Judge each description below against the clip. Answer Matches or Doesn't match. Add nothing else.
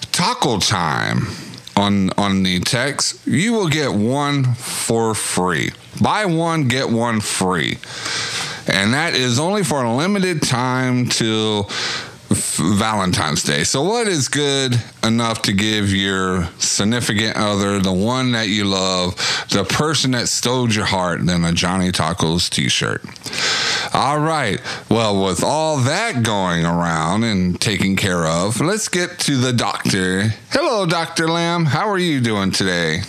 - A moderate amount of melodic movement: Doesn't match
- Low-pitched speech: Matches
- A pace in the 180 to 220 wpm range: Doesn't match